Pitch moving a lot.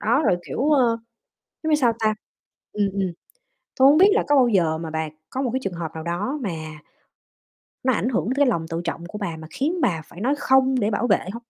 Yes: wide, 7.6 semitones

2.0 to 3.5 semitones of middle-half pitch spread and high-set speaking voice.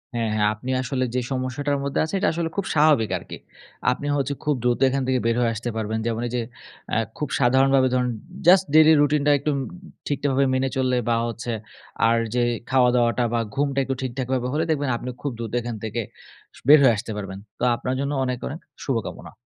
No: average, 3.1 semitones; low, 130 Hz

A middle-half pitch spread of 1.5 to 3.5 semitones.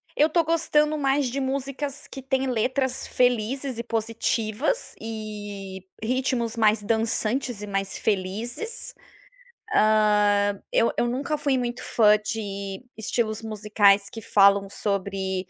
No: average, 4.3 semitones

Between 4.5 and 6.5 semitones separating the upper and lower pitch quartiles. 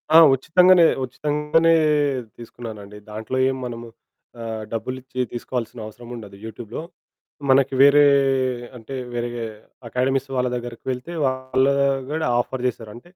No: average, 2.7 semitones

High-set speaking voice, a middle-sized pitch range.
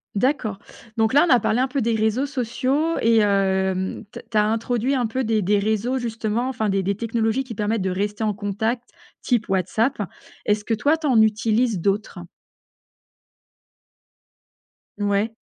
Yes: high, 220 Hz; average, 3.1 semitones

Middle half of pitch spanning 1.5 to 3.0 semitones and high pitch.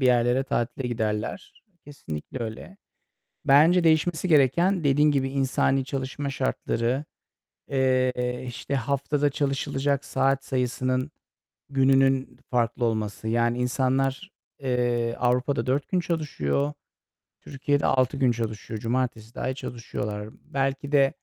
No: narrow, 2.5 semitones; low, 130 Hz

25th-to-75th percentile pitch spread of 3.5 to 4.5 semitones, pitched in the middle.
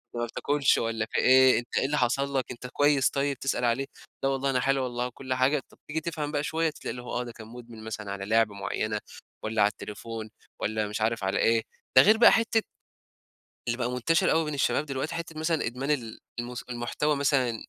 No: average, 3.9 semitones; low, 125 Hz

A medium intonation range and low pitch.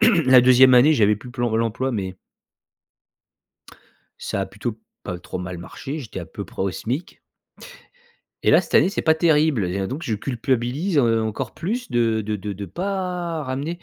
No: wide, 6.6 semitones; low, 125 Hz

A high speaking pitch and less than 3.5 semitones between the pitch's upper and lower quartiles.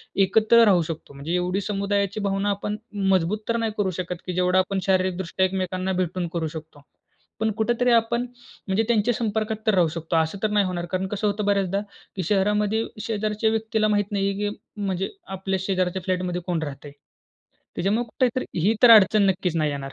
Yes: high, 195 Hz; average, 2.8 semitones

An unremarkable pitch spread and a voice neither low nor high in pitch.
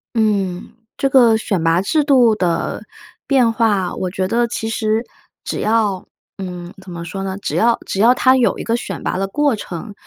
No: average, 4.0 semitones; high, 215 Hz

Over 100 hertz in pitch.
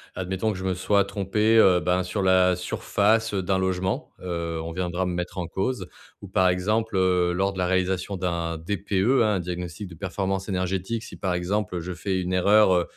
No: very low, 95 Hz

